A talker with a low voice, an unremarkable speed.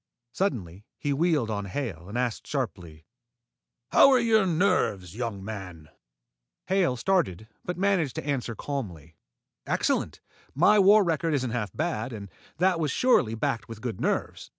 Yes: low, 125 Hz; average, 150 wpm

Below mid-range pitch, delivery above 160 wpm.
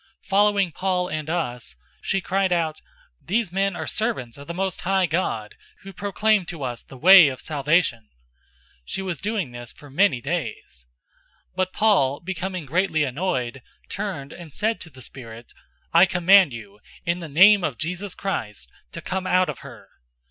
No: medium, 175 Hz; average, 170 wpm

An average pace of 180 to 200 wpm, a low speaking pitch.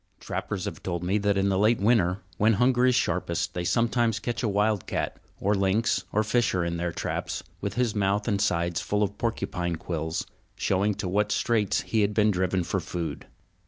Yes: average, 195 wpm; low, 100 Hz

